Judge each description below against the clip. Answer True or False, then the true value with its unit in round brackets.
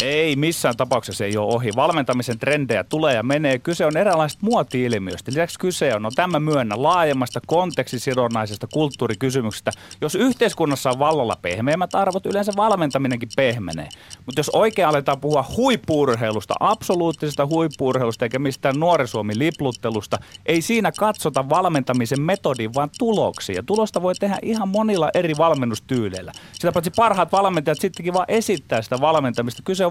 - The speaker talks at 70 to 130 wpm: False (140 wpm)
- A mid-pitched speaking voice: True (145 Hz)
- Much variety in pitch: True (6.1 semitones)